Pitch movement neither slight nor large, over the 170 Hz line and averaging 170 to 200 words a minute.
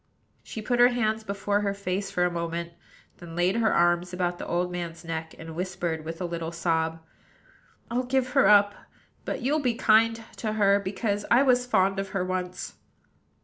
Yes: average, 4.1 semitones; high, 190 Hz; average, 190 wpm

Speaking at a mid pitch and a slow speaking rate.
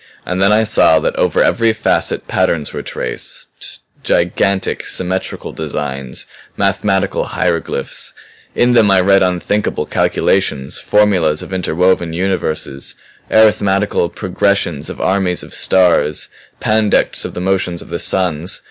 No: very low, 95 Hz; slow, 125 wpm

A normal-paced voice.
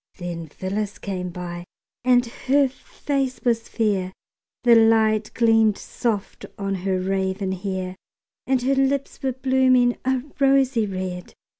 No: slow, 130 wpm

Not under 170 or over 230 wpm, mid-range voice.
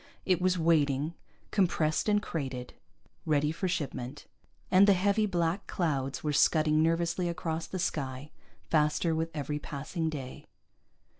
No: slow, 135 wpm; medium, 160 Hz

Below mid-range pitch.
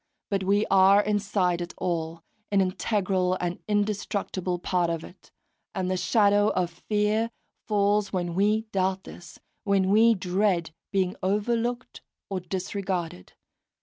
No: high, 195 Hz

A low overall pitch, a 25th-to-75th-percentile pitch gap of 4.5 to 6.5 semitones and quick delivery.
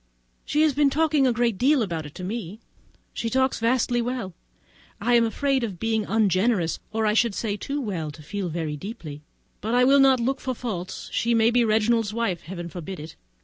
No: high, 225 Hz; average, 4.9 semitones; fast, 215 wpm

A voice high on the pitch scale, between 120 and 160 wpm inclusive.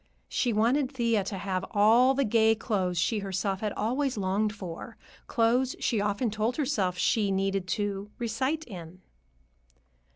Yes: high, 215 Hz; average, 150 wpm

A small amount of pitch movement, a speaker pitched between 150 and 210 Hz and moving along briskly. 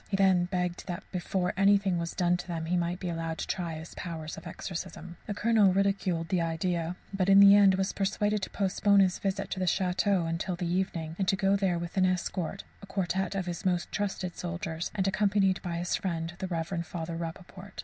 Yes: narrow, 2.3 semitones; medium, 185 Hz; fast, 215 wpm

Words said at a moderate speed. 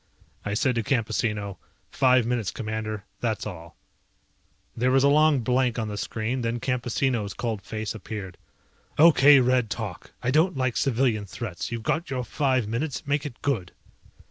Yes: average, 160 wpm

